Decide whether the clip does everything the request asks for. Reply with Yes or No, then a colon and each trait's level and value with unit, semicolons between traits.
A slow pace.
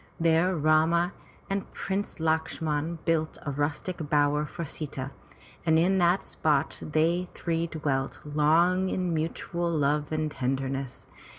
Yes: slow, 125 wpm